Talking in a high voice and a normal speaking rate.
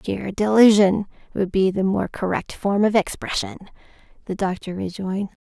Yes: high, 195 Hz; average, 145 wpm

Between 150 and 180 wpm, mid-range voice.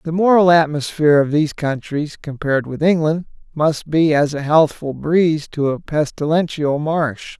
Yes: average, 155 wpm; medium, 155 Hz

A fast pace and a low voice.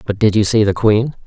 Yes: fast, 285 wpm; low, 110 Hz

